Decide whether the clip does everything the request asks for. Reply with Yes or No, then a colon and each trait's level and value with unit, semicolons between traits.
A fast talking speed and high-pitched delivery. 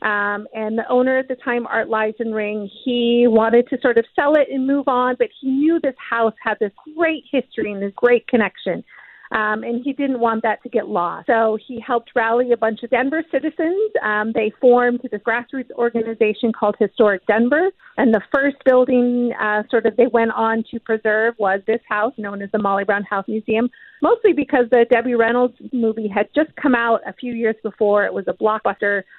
Yes: fast, 210 wpm; high, 235 Hz